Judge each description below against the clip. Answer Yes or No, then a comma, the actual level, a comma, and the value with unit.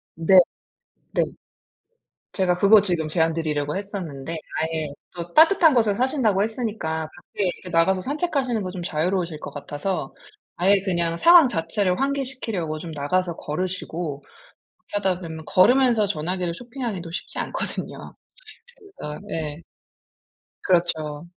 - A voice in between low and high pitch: Yes, medium, 180 Hz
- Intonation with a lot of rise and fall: No, average, 4.6 semitones